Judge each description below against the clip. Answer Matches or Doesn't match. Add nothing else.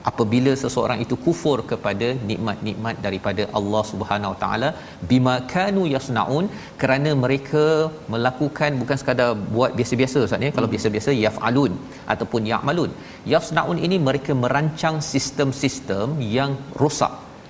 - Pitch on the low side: Matches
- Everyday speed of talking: Matches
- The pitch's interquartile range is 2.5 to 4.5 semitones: Doesn't match